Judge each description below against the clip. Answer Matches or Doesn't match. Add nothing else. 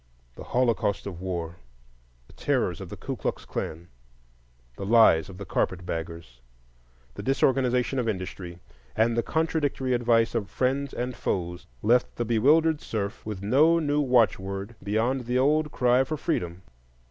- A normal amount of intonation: Doesn't match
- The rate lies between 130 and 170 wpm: Matches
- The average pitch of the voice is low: Matches